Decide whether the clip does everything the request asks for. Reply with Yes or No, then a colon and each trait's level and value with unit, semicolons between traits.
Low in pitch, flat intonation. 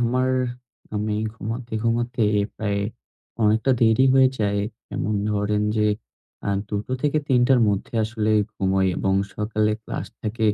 Yes: low, 110 Hz; narrow, 2.3 semitones